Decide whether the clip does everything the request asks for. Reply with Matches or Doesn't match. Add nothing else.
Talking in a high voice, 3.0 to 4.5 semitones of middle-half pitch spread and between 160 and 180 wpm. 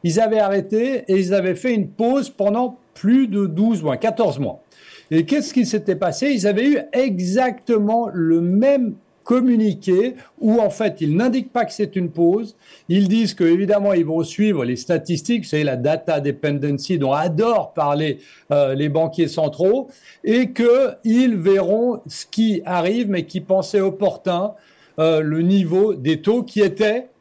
Doesn't match